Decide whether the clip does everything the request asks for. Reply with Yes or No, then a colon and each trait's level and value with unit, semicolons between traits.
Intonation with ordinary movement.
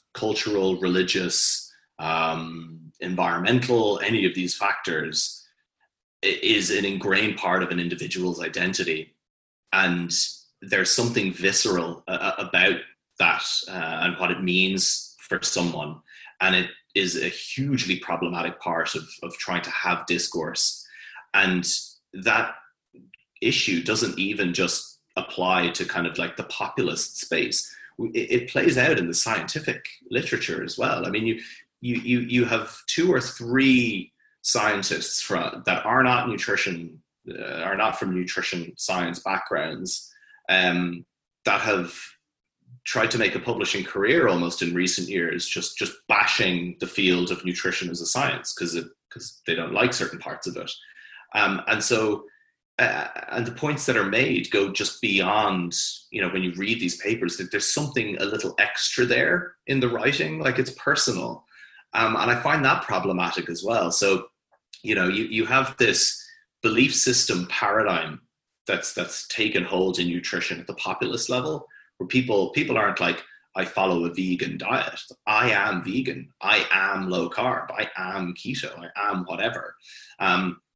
No: wide, 6.2 semitones